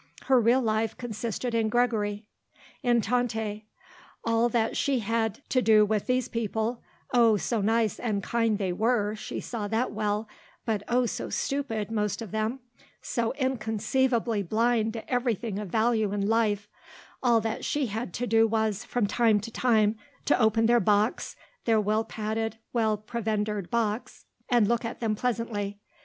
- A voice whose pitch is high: Yes, high, 225 Hz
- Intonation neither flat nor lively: No, narrow, 2.0 semitones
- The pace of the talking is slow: No, average, 160 wpm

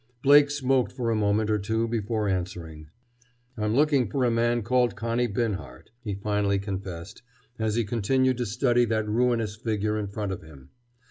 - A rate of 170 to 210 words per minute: Yes, average, 175 wpm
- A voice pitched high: No, low, 110 Hz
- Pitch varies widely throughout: No, average, 3.0 semitones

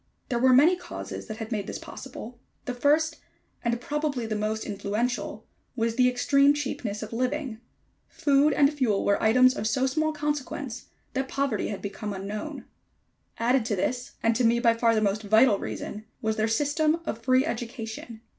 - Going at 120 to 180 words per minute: Yes, average, 175 wpm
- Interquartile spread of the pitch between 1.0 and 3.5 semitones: No, average, 4.0 semitones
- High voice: Yes, high, 245 Hz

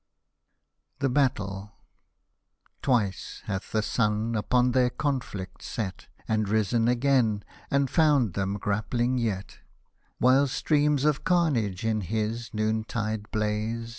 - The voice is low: Yes, low, 115 Hz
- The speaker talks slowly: Yes, slow, 110 wpm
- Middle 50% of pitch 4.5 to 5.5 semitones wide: No, average, 3.4 semitones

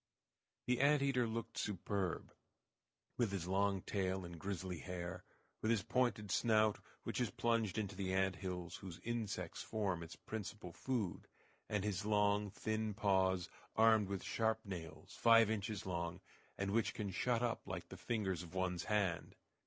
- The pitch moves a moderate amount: Yes, average, 3.1 semitones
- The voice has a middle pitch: No, low, 100 Hz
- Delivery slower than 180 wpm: Yes, average, 160 wpm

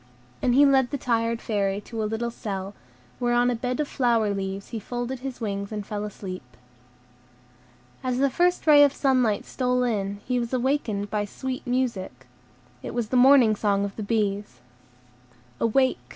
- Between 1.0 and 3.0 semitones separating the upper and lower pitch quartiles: No, average, 3.8 semitones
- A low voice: No, high, 235 Hz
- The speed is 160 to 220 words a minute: Yes, average, 175 wpm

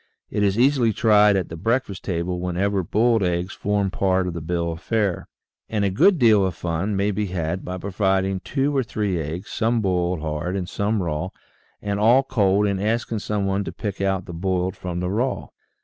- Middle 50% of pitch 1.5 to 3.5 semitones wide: Yes, average, 2.8 semitones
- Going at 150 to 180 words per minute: No, fast, 205 wpm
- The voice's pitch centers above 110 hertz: No, very low, 95 Hz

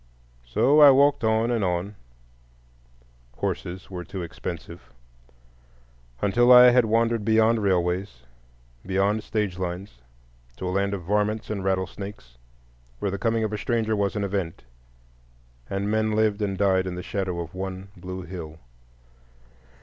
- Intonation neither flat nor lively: Yes, average, 4.7 semitones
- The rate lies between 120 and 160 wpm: Yes, slow, 135 wpm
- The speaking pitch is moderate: No, very low, 95 Hz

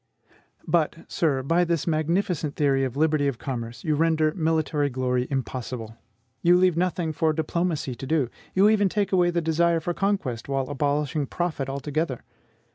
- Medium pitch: Yes, medium, 155 Hz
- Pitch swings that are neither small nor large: Yes, average, 4.0 semitones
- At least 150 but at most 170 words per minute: Yes, average, 160 wpm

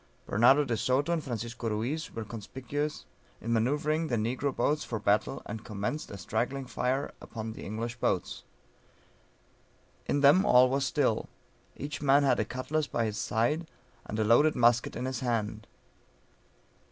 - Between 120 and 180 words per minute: Yes, average, 155 wpm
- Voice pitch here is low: Yes, low, 125 Hz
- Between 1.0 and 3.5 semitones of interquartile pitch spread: No, average, 4.2 semitones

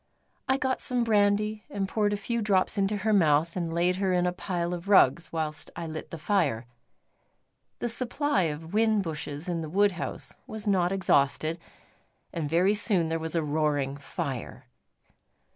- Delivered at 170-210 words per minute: Yes, average, 175 wpm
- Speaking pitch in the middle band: Yes, medium, 180 Hz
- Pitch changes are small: No, average, 4.2 semitones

